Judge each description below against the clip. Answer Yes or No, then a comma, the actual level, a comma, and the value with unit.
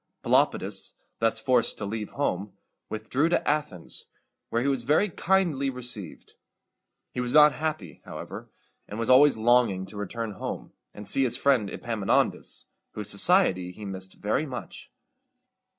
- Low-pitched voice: Yes, low, 115 Hz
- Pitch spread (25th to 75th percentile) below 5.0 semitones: No, average, 5.3 semitones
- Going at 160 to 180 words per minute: No, average, 145 wpm